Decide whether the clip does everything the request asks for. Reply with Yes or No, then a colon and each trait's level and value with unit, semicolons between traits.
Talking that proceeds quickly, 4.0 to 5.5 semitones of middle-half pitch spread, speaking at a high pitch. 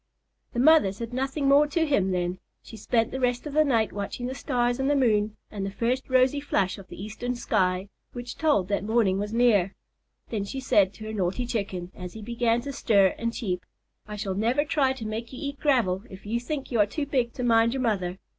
Yes: fast, 230 wpm; average, 4.5 semitones; high, 230 Hz